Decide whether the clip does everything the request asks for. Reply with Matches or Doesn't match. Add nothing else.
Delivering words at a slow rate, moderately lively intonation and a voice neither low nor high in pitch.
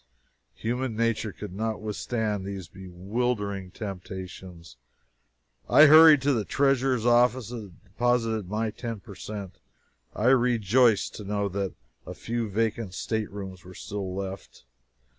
Doesn't match